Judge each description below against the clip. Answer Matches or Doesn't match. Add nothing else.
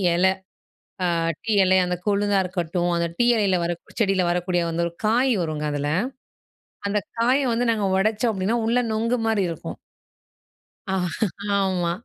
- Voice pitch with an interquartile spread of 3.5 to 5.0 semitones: Matches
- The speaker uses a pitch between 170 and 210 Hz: Matches